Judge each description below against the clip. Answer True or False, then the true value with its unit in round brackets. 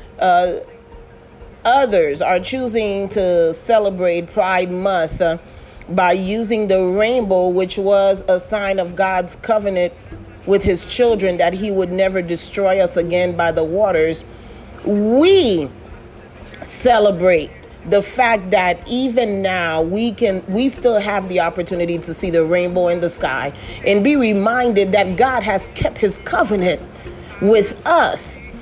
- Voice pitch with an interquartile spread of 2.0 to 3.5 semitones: True (3.2 semitones)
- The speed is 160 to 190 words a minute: False (135 wpm)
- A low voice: False (190 Hz)